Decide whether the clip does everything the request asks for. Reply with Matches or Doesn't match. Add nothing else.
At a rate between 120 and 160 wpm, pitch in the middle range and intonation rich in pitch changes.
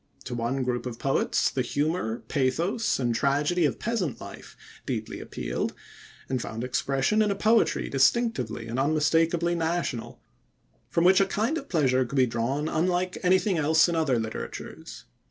Matches